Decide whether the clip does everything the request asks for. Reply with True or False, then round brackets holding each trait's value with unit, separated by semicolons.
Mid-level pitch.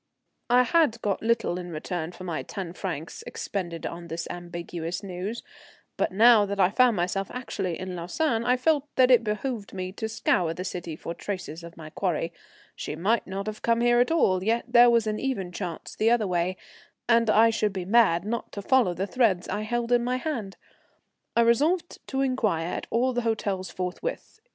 False (205 Hz)